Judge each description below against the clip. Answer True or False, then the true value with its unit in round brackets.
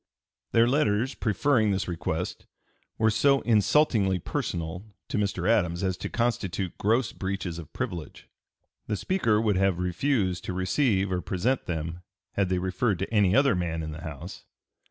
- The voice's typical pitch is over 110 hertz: False (95 Hz)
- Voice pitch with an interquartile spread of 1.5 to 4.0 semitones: False (4.4 semitones)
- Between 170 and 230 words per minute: False (155 wpm)